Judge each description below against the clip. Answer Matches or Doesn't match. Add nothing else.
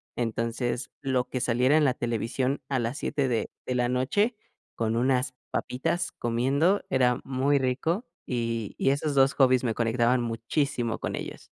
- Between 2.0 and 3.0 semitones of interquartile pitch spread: Matches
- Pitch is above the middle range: Doesn't match